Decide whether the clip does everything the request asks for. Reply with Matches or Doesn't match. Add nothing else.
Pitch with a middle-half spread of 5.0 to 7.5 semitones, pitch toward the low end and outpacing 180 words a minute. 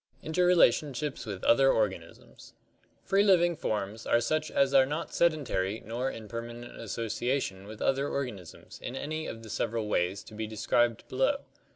Doesn't match